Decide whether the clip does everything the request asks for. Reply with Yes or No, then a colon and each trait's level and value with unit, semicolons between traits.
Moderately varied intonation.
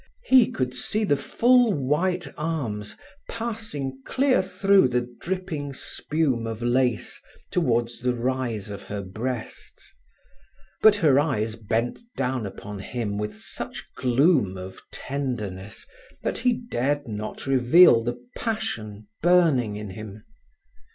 No: wide, 7.8 semitones